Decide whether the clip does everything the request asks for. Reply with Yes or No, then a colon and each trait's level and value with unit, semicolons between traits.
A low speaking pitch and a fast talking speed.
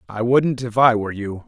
Yes: low, 115 Hz; fast, 285 wpm